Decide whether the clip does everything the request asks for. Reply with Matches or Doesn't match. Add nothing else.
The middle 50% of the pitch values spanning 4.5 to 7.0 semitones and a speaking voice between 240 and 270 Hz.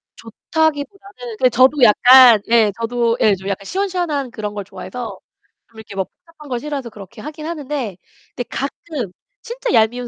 Matches